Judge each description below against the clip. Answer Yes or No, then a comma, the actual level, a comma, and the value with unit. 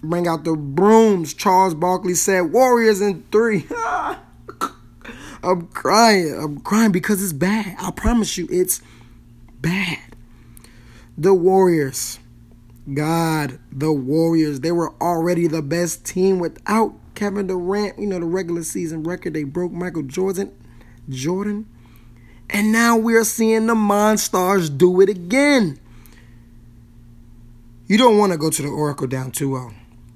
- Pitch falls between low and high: Yes, medium, 170 Hz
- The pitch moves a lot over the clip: Yes, wide, 7.3 semitones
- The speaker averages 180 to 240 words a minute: No, slow, 135 wpm